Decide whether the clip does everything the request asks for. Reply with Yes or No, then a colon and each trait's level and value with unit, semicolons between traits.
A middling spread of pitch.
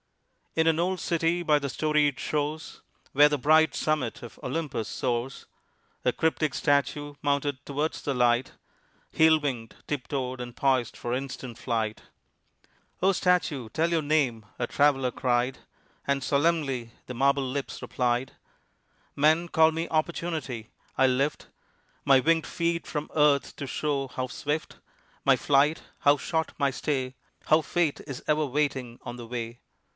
Yes: average, 3.4 semitones